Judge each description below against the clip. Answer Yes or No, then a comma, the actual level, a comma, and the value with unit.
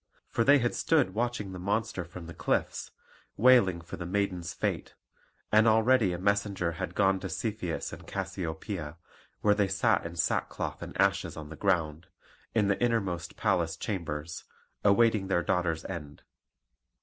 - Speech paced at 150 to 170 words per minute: Yes, average, 155 wpm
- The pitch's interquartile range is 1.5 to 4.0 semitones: Yes, average, 3.7 semitones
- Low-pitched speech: Yes, very low, 95 Hz